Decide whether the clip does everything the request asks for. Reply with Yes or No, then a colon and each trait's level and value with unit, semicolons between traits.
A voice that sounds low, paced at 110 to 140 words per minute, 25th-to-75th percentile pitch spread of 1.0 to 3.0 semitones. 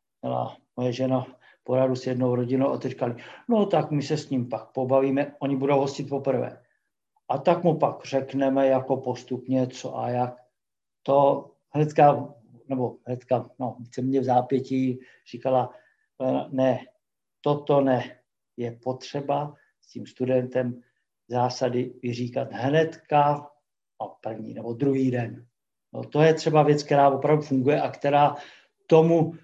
Yes: low, 130 Hz; slow, 135 wpm; narrow, 2.5 semitones